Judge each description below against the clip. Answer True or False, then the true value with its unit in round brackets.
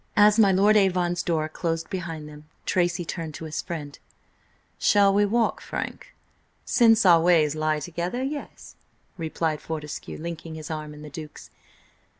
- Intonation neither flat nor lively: True (3.8 semitones)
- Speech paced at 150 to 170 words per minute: True (155 wpm)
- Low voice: False (170 Hz)